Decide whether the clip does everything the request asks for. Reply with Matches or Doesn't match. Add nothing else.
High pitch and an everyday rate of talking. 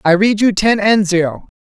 Doesn't match